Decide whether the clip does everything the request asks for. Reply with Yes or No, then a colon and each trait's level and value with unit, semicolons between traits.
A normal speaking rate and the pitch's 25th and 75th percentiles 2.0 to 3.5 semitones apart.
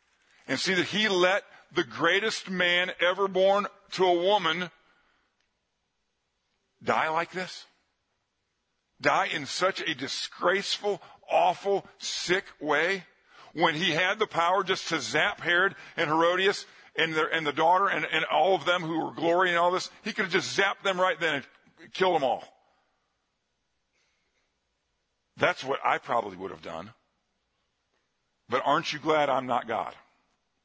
Yes: average, 150 wpm; average, 3.0 semitones